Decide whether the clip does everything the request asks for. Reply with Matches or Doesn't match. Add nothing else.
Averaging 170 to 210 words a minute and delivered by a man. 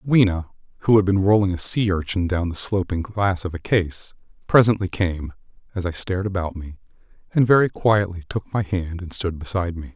Matches